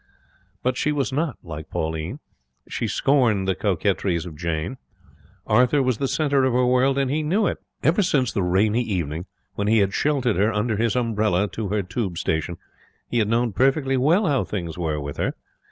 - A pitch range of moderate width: No, wide, 6.6 semitones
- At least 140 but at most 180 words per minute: No, average, 190 wpm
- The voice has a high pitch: No, low, 110 Hz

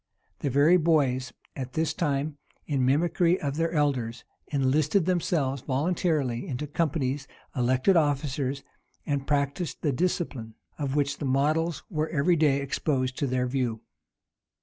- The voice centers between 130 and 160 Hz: Yes, medium, 140 Hz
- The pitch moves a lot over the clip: No, average, 3.2 semitones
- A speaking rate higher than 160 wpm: No, slow, 135 wpm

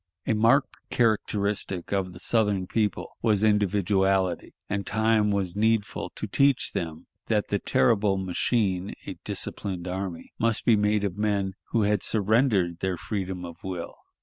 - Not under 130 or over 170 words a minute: Yes, average, 150 wpm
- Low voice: Yes, low, 100 Hz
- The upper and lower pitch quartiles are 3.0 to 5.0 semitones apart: No, narrow, 2.6 semitones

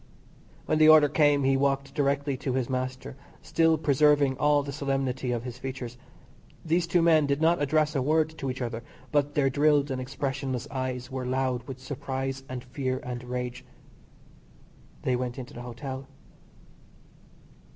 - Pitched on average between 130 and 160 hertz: Yes, low, 135 Hz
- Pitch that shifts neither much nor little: No, narrow, 2.3 semitones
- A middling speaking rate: Yes, average, 160 wpm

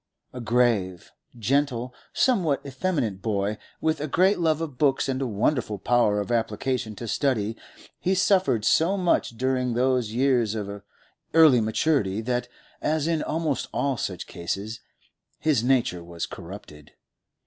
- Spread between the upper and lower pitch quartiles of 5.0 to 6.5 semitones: Yes, wide, 5.5 semitones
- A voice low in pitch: Yes, low, 125 Hz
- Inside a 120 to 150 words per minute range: Yes, average, 140 wpm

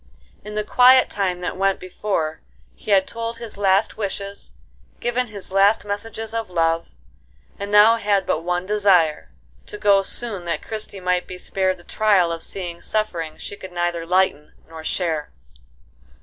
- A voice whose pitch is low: No, high, 195 Hz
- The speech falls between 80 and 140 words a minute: No, average, 160 wpm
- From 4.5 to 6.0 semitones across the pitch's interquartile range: No, average, 3.0 semitones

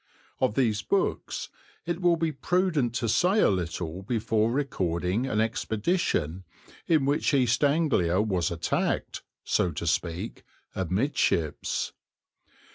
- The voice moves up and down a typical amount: No, wide, 8.1 semitones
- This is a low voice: Yes, low, 115 Hz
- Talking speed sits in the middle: No, slow, 120 wpm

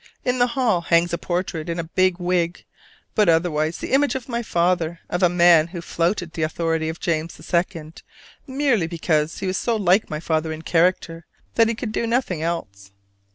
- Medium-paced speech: Yes, average, 195 wpm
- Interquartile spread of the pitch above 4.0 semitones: No, average, 3.2 semitones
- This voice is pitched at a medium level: Yes, medium, 170 Hz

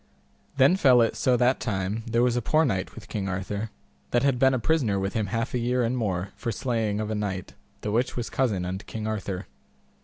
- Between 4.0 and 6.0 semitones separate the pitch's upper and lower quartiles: No, average, 3.6 semitones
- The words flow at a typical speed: No, fast, 220 wpm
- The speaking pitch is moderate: No, low, 115 Hz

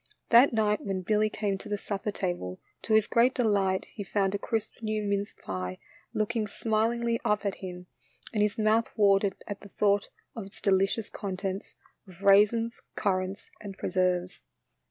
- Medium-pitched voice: No, high, 205 Hz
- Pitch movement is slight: Yes, narrow, 2.0 semitones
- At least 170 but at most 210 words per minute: Yes, average, 175 wpm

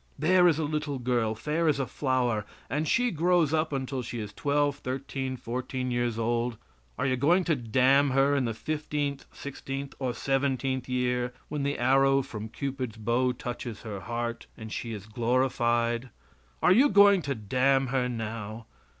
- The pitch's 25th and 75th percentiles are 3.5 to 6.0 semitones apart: No, average, 3.1 semitones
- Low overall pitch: Yes, low, 130 Hz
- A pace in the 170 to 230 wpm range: Yes, average, 175 wpm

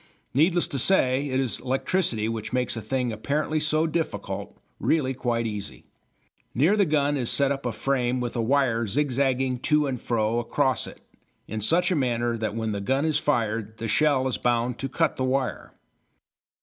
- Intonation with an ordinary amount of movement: Yes, average, 3.8 semitones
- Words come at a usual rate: Yes, average, 185 wpm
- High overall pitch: No, low, 130 Hz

